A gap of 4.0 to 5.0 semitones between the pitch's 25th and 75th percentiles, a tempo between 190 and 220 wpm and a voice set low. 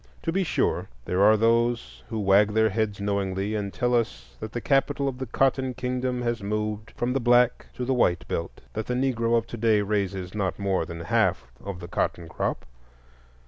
No: average, 3.6 semitones; average, 195 wpm; low, 110 Hz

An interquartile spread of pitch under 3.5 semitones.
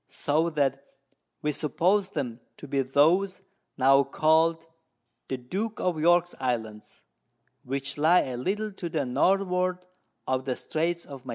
No: average, 5.0 semitones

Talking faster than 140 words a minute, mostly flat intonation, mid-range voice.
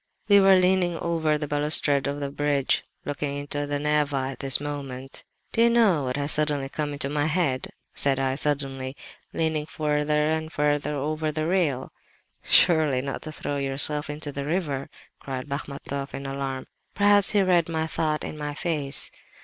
Yes: average, 170 wpm; narrow, 2.2 semitones; medium, 145 Hz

